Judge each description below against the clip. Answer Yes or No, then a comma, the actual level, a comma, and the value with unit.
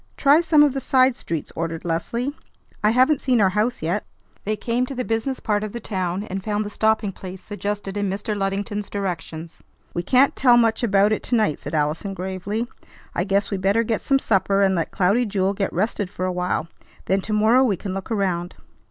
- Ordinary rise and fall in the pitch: Yes, average, 3.5 semitones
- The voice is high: Yes, high, 205 Hz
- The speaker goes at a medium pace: No, fast, 215 wpm